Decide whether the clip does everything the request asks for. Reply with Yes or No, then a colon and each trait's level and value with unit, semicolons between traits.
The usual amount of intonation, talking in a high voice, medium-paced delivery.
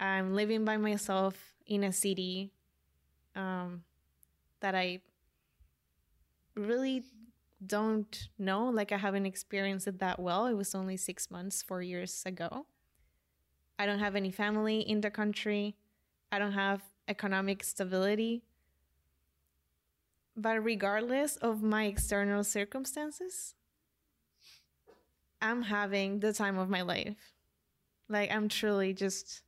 No: average, 3.0 semitones; high, 195 Hz; slow, 120 wpm